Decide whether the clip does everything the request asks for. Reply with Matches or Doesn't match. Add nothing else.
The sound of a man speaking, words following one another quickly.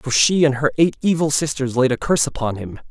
Matches